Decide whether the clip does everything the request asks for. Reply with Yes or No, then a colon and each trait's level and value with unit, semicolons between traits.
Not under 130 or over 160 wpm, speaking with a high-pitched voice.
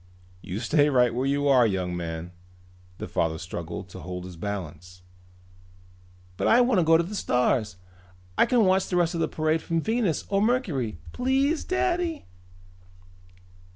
No: average, 155 wpm; medium, 140 Hz